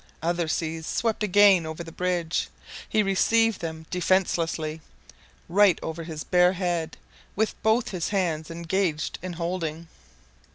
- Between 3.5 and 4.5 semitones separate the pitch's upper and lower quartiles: No, average, 3.0 semitones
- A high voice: No, medium, 175 Hz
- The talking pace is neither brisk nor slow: No, slow, 130 wpm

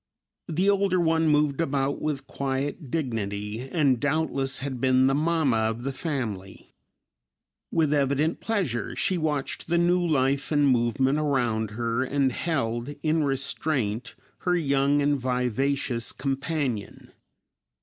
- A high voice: No, medium, 140 Hz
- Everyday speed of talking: No, slow, 130 wpm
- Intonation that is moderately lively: Yes, average, 3.7 semitones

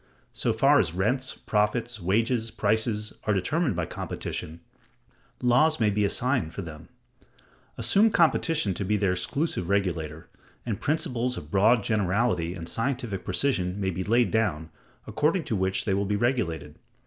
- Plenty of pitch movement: No, average, 4.9 semitones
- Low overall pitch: Yes, low, 105 Hz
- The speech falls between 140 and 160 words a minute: Yes, average, 150 wpm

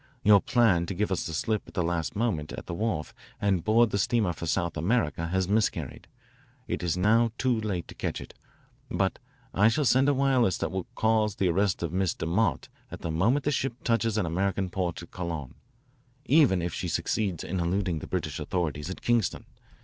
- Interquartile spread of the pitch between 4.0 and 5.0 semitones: Yes, average, 4.5 semitones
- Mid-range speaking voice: No, very low, 95 Hz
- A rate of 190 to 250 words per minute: Yes, average, 200 wpm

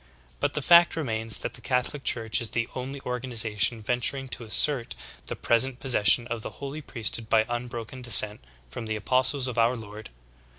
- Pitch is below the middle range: Yes, low, 120 Hz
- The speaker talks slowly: No, average, 180 wpm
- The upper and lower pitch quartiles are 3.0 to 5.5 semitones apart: No, narrow, 2.5 semitones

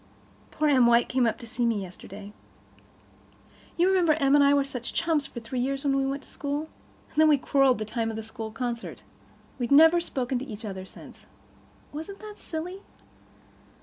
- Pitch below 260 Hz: No, very high, 270 Hz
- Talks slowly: No, average, 195 wpm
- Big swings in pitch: No, average, 4.4 semitones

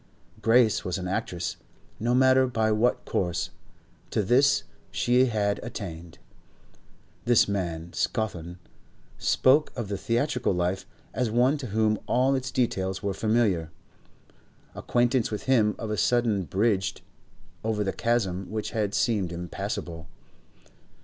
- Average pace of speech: No, slow, 130 wpm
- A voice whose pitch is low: Yes, low, 110 Hz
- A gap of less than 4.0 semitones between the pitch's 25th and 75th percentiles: No, average, 4.3 semitones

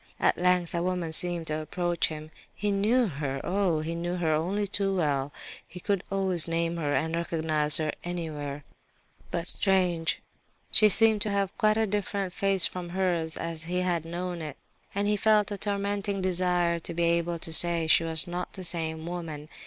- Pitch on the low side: No, medium, 175 Hz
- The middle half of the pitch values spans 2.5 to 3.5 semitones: Yes, average, 3.0 semitones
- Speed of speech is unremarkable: Yes, average, 185 wpm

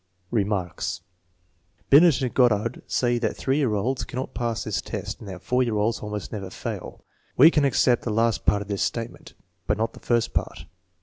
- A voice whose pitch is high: No, low, 115 Hz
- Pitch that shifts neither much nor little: Yes, average, 3.2 semitones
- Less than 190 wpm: No, average, 195 wpm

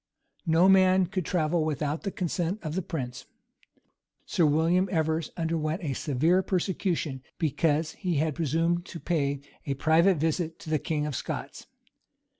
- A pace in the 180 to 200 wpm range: No, average, 155 wpm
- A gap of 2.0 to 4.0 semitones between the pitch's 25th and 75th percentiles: Yes, narrow, 2.6 semitones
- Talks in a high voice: No, medium, 160 Hz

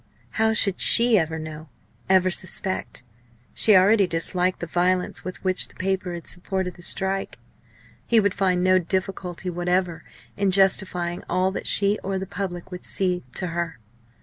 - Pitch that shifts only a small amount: Yes, narrow, 1.5 semitones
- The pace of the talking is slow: No, average, 160 wpm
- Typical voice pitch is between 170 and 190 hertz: Yes, medium, 185 Hz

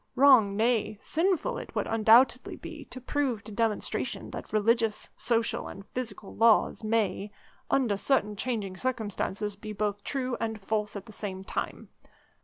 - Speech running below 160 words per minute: Yes, average, 150 wpm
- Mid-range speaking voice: No, high, 220 Hz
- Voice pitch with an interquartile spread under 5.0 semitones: Yes, average, 3.0 semitones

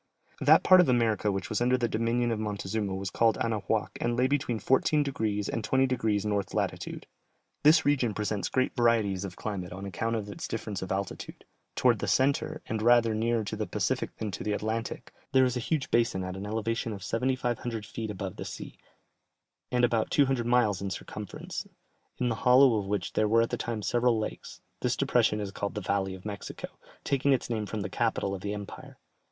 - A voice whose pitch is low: Yes, low, 110 Hz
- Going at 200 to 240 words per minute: Yes, fast, 205 wpm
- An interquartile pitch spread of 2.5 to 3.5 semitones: Yes, average, 3.0 semitones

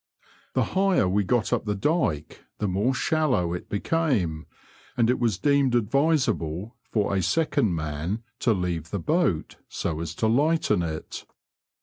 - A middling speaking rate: Yes, average, 150 wpm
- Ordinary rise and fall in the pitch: No, wide, 8.2 semitones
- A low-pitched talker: Yes, low, 105 Hz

